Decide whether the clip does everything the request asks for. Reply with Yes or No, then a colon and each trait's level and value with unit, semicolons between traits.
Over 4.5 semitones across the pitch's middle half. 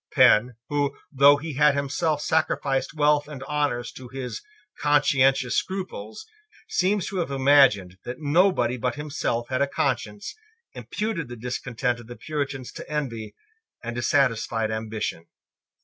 No: average, 3.5 semitones